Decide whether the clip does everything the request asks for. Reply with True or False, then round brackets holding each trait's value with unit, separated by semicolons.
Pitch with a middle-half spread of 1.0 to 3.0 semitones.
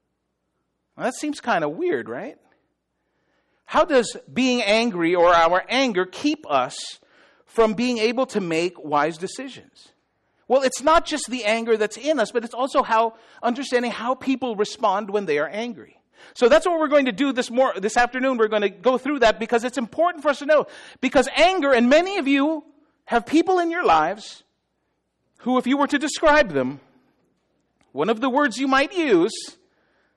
False (4.8 semitones)